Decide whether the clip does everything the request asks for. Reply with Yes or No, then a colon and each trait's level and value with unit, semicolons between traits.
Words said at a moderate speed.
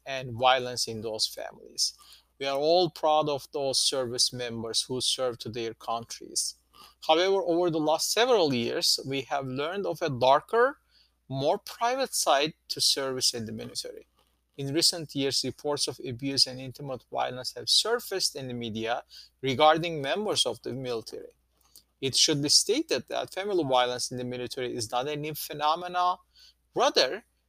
Yes: average, 160 wpm